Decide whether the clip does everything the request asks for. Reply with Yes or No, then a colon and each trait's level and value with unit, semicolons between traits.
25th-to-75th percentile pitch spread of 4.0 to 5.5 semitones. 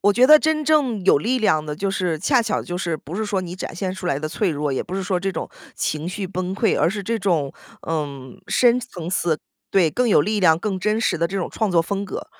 Yes: average, 4.3 semitones